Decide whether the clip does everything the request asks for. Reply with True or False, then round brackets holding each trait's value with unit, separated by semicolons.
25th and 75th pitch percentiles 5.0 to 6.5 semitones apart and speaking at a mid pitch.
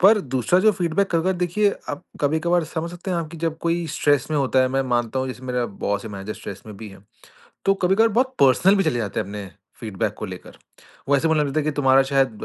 True (5.5 semitones; 145 Hz)